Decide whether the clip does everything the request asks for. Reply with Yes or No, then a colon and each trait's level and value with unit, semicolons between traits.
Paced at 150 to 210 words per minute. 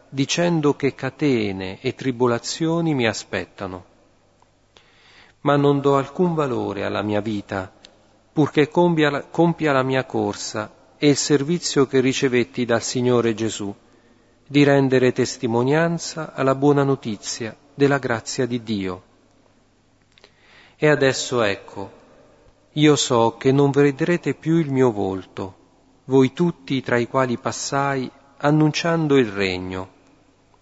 No: average, 120 wpm